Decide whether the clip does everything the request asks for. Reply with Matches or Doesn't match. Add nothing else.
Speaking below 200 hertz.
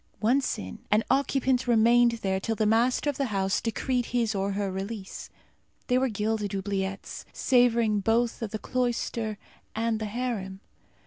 Doesn't match